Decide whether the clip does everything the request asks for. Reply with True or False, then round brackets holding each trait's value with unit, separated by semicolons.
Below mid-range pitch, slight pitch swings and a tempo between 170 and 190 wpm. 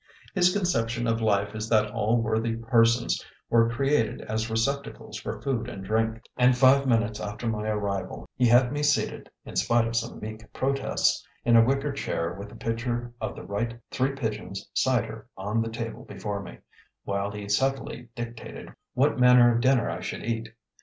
True (115 Hz; 2.3 semitones; 180 wpm)